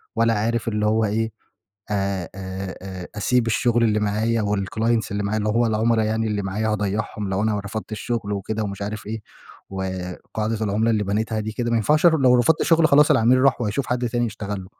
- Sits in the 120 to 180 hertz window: No, low, 110 Hz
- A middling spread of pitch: No, narrow, 2.2 semitones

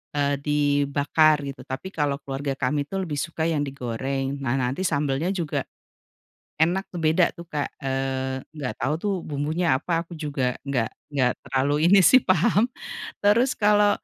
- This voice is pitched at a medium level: Yes, medium, 145 Hz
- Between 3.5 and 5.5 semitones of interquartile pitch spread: Yes, average, 3.9 semitones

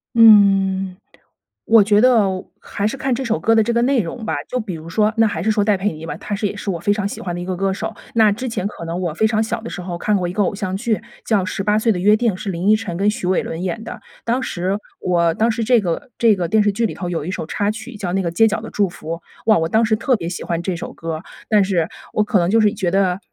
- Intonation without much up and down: No, average, 3.6 semitones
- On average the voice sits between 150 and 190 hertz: No, high, 205 Hz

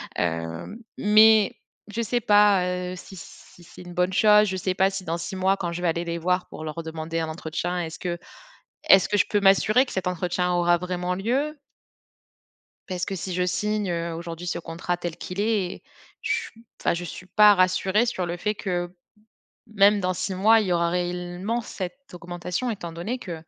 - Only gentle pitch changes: No, average, 3.0 semitones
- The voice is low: No, medium, 180 Hz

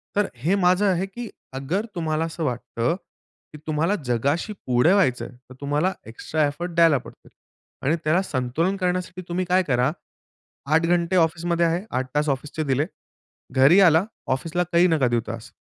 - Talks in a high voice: No, medium, 160 Hz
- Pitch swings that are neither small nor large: Yes, average, 4.8 semitones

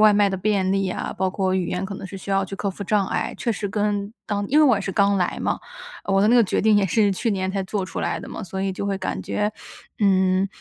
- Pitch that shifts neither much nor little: No, narrow, 1.5 semitones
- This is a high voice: Yes, high, 195 Hz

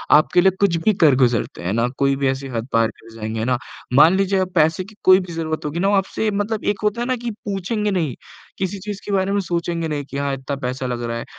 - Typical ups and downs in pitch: No, wide, 6.8 semitones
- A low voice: No, medium, 165 Hz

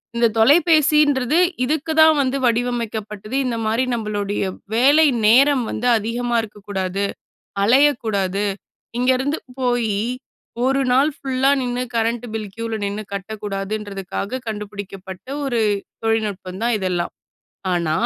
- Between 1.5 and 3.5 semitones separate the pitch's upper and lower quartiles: No, average, 4.1 semitones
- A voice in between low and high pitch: No, high, 225 Hz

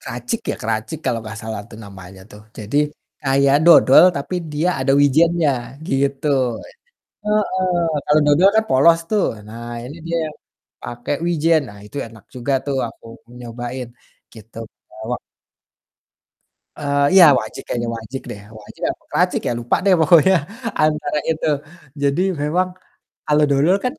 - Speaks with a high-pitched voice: No, medium, 140 Hz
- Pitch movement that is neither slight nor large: No, wide, 5.8 semitones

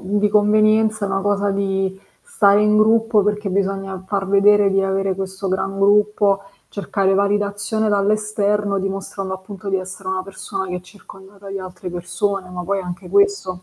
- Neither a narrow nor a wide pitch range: No, narrow, 1.4 semitones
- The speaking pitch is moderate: No, high, 195 Hz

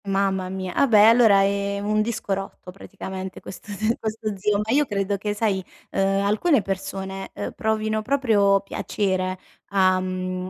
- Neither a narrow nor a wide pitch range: No, narrow, 2.0 semitones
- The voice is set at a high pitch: Yes, high, 200 Hz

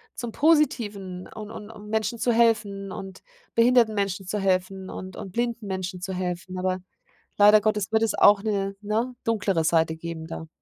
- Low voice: No, high, 205 Hz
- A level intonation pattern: No, average, 3.0 semitones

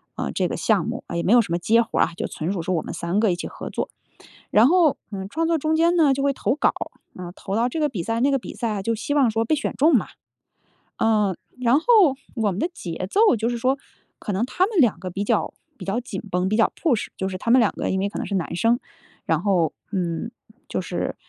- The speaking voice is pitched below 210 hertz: No, high, 225 Hz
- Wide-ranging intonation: Yes, wide, 6.2 semitones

